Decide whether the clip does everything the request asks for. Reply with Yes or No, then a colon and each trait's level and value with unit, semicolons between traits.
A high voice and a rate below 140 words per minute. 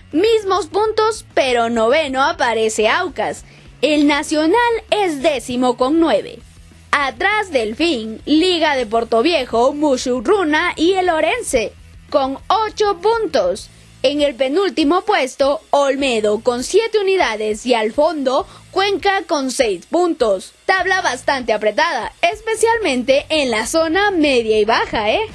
Yes: very high, 305 Hz; slow, 125 wpm